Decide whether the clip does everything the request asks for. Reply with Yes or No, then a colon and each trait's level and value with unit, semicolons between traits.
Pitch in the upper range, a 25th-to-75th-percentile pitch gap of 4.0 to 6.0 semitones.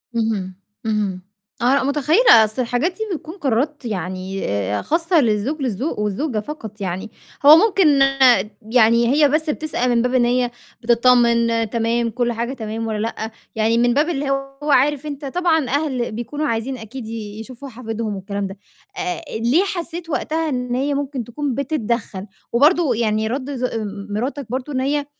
Yes: high, 245 Hz; average, 4.6 semitones